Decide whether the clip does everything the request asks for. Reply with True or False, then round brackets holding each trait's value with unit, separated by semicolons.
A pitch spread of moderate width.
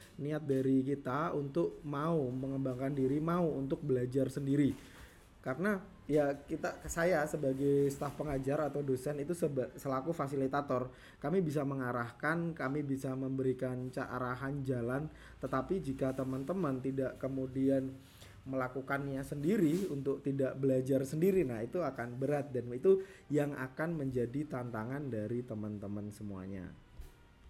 False (2.3 semitones)